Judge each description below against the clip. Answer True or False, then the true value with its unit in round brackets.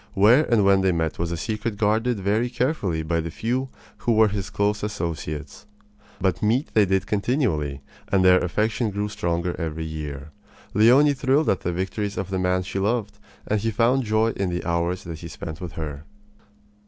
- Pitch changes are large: False (4.5 semitones)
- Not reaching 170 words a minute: False (190 wpm)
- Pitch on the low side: True (100 Hz)